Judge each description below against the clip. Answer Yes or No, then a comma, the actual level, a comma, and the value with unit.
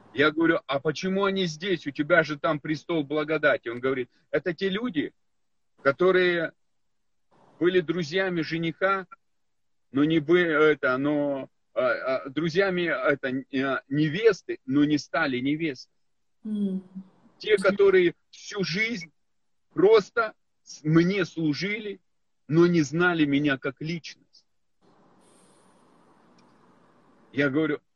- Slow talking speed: Yes, slow, 105 wpm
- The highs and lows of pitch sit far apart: No, average, 4.5 semitones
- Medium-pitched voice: Yes, medium, 165 Hz